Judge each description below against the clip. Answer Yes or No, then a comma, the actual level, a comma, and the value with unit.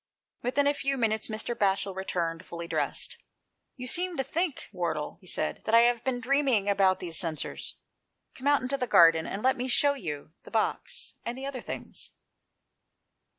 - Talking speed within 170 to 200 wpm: Yes, average, 190 wpm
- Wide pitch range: Yes, wide, 6.5 semitones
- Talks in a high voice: Yes, high, 230 Hz